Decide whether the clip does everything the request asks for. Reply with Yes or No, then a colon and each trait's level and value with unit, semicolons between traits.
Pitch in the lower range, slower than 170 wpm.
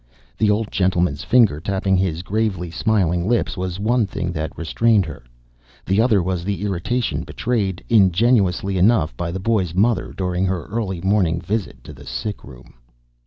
Yes: very low, 95 Hz; average, 160 wpm